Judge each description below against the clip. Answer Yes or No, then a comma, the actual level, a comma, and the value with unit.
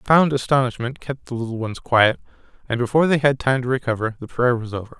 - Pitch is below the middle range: Yes, low, 125 Hz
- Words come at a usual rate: No, fast, 215 wpm